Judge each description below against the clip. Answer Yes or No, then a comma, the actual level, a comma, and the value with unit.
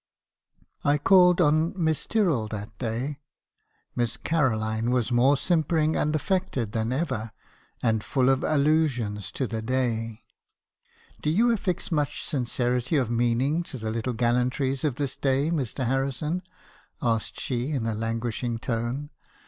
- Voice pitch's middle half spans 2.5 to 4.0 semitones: No, average, 4.5 semitones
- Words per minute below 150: Yes, average, 140 wpm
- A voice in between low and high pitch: No, low, 130 Hz